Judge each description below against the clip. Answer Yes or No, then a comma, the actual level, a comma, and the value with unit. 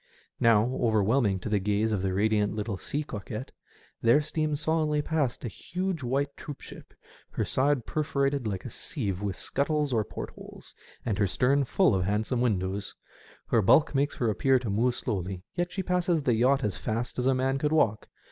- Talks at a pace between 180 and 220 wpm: Yes, average, 190 wpm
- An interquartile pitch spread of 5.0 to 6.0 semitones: Yes, wide, 5.6 semitones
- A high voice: No, low, 120 Hz